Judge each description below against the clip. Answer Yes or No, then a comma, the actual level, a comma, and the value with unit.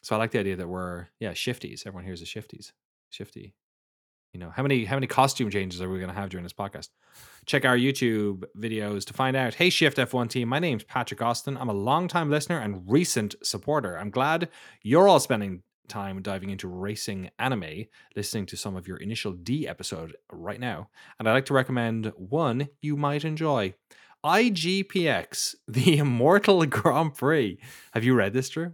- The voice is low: Yes, low, 120 Hz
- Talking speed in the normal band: Yes, average, 190 wpm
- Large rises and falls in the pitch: Yes, wide, 6.3 semitones